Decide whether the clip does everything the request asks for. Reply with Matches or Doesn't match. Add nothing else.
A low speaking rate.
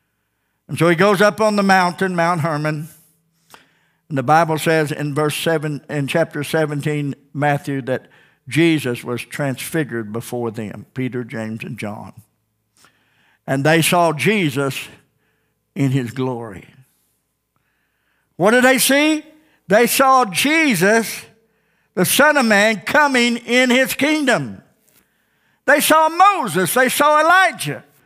Matches